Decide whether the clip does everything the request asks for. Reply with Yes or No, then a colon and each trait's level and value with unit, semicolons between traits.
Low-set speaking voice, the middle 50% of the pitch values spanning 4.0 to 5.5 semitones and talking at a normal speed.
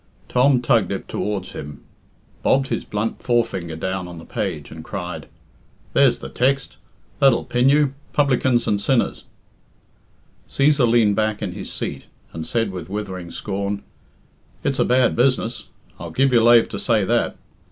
Yes: low, 110 Hz; average, 5.0 semitones; average, 150 wpm